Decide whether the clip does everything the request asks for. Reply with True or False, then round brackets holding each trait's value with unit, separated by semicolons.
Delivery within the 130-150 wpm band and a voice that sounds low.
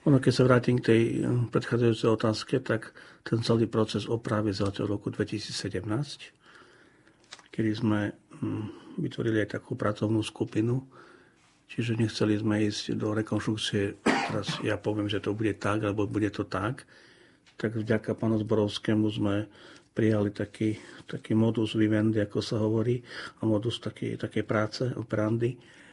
True (135 wpm; 110 Hz)